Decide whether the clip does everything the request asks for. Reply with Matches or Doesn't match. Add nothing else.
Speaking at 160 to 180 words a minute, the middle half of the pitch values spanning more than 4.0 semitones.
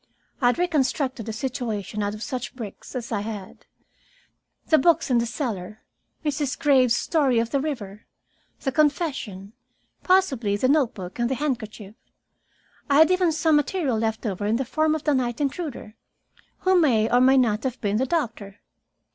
Matches